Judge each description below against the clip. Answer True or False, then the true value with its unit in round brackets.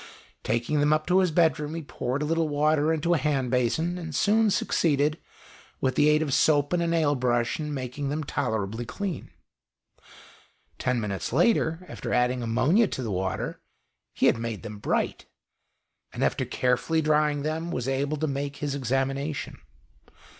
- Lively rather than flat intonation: False (4.0 semitones)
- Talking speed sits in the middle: True (170 wpm)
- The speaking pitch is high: False (145 Hz)